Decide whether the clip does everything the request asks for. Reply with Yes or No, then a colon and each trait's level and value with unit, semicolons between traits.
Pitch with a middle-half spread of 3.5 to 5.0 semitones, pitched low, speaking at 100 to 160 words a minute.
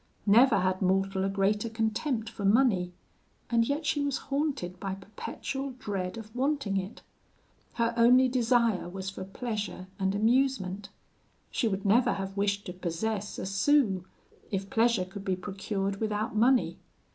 No: average, 3.8 semitones; high, 210 Hz; average, 150 wpm